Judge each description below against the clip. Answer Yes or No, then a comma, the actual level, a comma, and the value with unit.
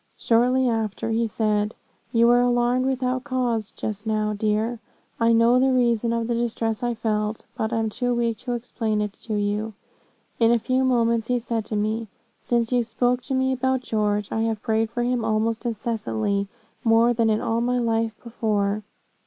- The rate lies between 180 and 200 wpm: Yes, average, 185 wpm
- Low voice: No, high, 230 Hz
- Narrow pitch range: Yes, narrow, 1.9 semitones